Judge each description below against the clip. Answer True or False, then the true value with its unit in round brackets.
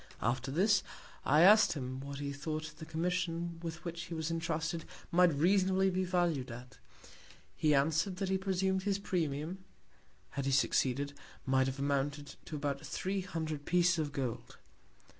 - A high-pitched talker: False (160 Hz)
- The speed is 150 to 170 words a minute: True (160 wpm)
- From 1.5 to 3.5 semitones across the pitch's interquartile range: False (4.2 semitones)